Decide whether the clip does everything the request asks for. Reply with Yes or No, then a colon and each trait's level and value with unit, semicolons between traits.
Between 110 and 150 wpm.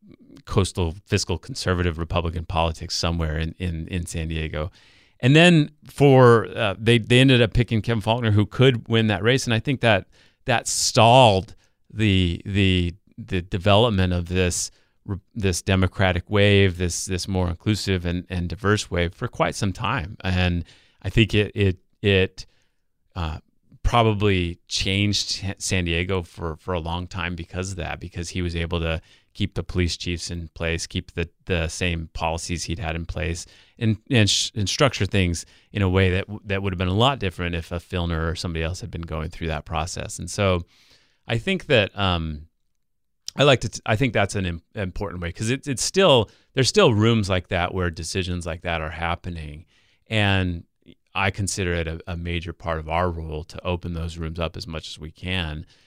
No: average, 190 wpm